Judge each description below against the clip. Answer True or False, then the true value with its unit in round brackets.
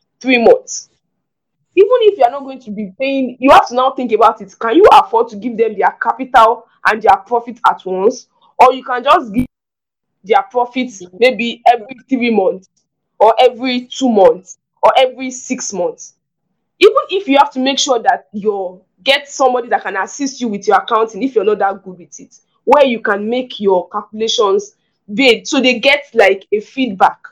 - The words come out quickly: False (195 wpm)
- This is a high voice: True (250 Hz)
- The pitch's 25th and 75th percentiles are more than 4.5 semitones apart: False (4.2 semitones)